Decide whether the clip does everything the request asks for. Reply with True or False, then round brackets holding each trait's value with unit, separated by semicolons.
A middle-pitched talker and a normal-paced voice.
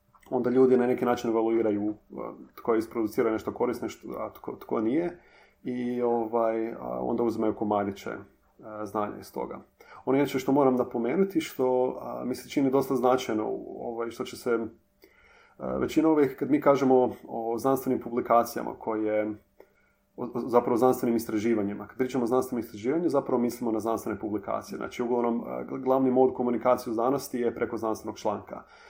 False (120 Hz; 150 wpm)